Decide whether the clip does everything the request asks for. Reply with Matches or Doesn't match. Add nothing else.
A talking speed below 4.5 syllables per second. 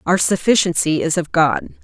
Doesn't match